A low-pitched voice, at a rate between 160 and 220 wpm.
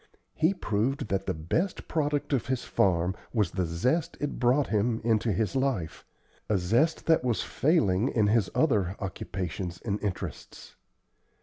No: low, 110 Hz; average, 150 wpm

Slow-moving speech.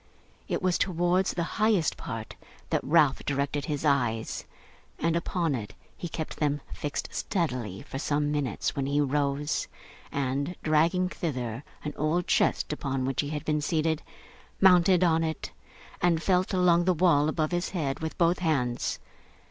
No: average, 155 wpm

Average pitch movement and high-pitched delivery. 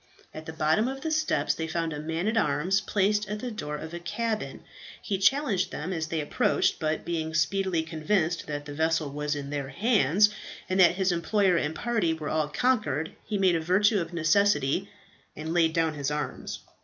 No: average, 4.5 semitones; medium, 165 Hz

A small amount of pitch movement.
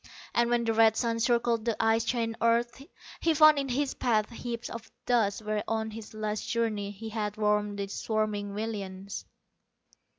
Yes: narrow, 1.9 semitones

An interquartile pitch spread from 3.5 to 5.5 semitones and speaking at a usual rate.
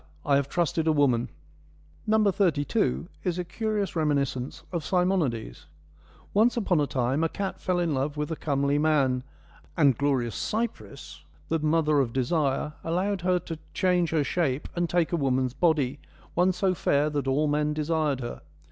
Yes: average, 4.2 semitones; average, 165 wpm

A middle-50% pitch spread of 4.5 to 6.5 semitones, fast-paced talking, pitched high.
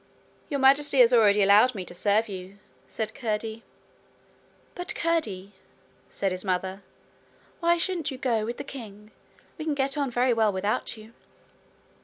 No: average, 5.0 semitones; average, 155 wpm; high, 225 Hz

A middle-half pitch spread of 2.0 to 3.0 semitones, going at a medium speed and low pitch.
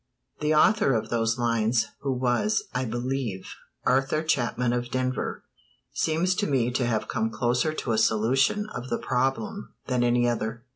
Yes: narrow, 2.4 semitones; average, 160 wpm; low, 125 Hz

